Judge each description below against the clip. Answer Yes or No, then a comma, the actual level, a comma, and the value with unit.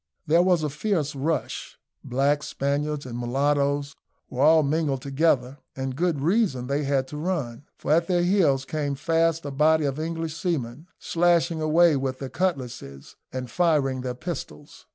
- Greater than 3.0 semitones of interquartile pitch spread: Yes, average, 3.5 semitones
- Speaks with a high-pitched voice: No, medium, 145 Hz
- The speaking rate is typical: Yes, average, 160 wpm